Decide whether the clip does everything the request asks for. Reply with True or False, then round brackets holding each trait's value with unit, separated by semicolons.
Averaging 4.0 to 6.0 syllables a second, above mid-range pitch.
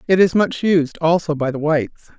False (5.5 syllables/s; 170 Hz)